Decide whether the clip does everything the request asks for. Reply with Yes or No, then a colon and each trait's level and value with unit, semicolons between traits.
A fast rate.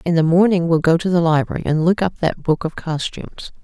Yes: fast, 245 wpm